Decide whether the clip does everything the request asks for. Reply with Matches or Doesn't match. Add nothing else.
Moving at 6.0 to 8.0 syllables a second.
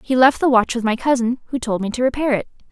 Matches